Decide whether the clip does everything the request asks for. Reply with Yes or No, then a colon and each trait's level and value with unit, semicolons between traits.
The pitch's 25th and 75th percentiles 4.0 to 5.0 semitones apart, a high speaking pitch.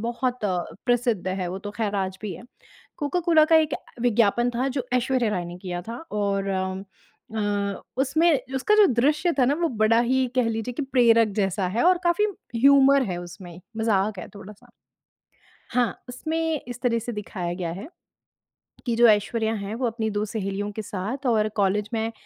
Yes: average, 4.3 semitones; high, 225 Hz